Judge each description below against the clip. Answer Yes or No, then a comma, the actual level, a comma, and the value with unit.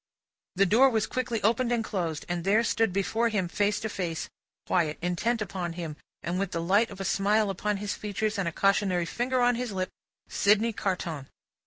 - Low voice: No, high, 200 Hz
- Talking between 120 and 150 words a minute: No, average, 190 wpm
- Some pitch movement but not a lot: Yes, average, 3.9 semitones